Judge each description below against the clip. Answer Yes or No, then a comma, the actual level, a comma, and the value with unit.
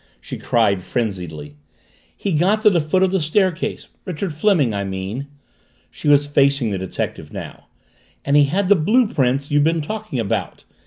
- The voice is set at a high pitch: No, medium, 145 Hz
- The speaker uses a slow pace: No, average, 175 wpm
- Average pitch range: No, wide, 8.4 semitones